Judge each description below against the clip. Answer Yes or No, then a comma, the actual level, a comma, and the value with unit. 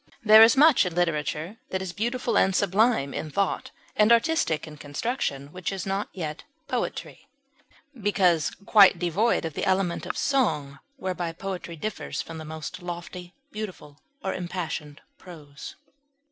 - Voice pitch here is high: No, medium, 180 Hz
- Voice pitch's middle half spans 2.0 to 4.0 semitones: No, average, 4.8 semitones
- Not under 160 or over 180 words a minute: No, average, 145 wpm